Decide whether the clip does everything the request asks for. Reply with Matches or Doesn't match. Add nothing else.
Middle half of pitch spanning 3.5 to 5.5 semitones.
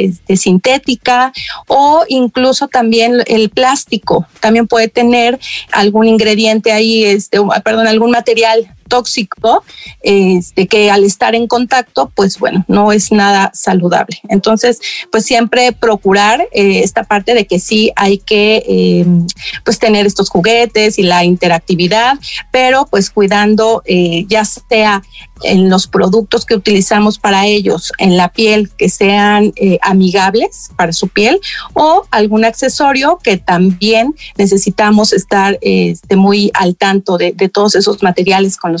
Doesn't match